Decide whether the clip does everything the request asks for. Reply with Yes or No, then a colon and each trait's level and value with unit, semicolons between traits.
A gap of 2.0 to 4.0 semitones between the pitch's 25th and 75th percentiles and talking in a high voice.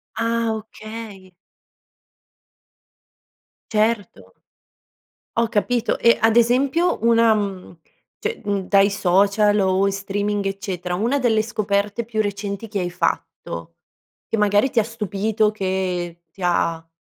Yes: average, 2.7 semitones; high, 205 Hz